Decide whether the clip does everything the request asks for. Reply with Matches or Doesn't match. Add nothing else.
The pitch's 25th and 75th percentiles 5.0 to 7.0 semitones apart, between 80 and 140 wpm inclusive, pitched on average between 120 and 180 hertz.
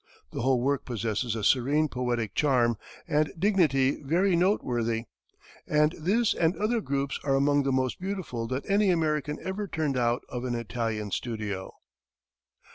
Doesn't match